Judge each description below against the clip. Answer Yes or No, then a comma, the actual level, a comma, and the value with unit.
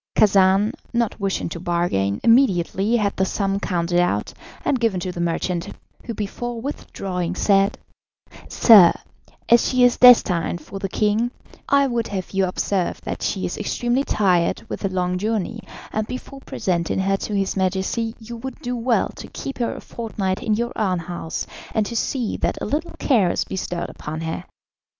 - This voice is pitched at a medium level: No, high, 200 Hz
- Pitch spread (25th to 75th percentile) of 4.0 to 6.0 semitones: Yes, average, 4.4 semitones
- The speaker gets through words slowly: No, average, 175 wpm